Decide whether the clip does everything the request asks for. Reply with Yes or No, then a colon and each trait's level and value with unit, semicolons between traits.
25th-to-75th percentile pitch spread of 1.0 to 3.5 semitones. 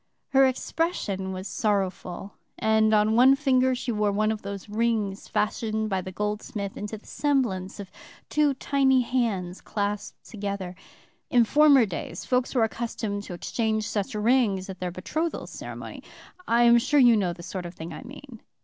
No: average, 4.2 semitones